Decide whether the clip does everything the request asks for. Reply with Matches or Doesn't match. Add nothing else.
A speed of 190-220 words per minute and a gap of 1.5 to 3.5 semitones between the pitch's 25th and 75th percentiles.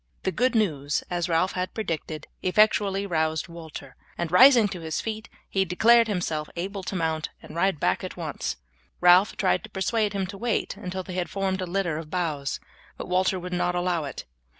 Matches